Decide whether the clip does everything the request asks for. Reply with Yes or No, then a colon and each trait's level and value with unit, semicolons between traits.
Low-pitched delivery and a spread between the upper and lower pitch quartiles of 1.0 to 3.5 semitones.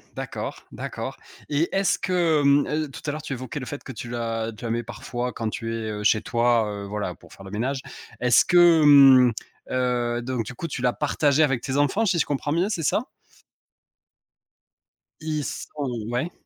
No: low, 130 Hz; average, 4.2 semitones